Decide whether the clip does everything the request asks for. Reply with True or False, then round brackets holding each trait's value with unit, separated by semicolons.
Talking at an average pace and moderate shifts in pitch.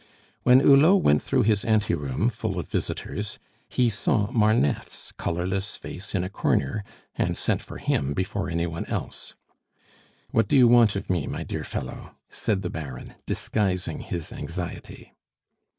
True (150 wpm; 4.5 semitones)